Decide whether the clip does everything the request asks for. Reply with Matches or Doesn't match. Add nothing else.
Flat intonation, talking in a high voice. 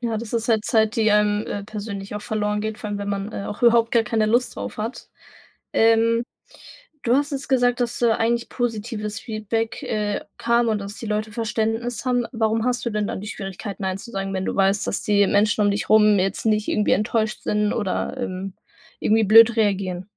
Matches